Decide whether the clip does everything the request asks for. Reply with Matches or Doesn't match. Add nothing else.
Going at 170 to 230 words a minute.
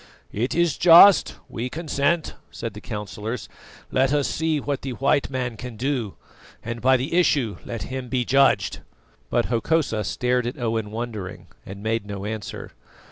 Doesn't match